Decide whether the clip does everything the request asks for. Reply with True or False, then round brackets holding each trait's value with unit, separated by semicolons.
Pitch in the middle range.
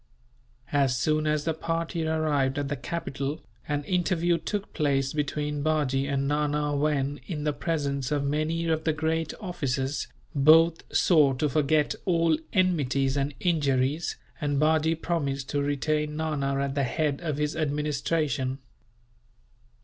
True (150 Hz)